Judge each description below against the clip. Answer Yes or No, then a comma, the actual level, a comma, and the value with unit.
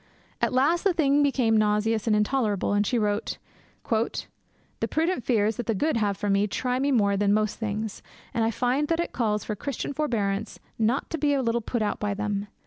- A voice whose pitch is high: Yes, high, 225 Hz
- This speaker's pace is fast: Yes, fast, 210 wpm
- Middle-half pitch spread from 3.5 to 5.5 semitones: Yes, average, 4.3 semitones